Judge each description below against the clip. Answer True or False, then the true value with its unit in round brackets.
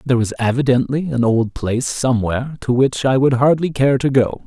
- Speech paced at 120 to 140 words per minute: False (200 wpm)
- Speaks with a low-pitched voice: True (130 Hz)